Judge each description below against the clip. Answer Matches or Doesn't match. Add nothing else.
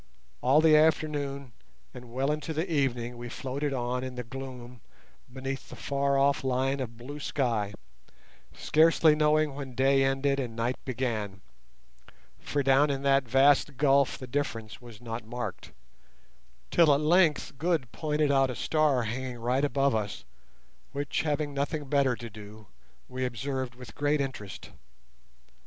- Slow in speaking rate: Doesn't match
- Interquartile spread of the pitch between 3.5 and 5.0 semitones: Doesn't match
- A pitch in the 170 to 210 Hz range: Doesn't match